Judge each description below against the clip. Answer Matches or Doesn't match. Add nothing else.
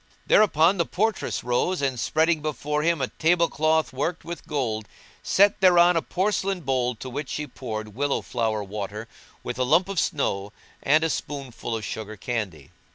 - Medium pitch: Matches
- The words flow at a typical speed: Matches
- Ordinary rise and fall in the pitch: Doesn't match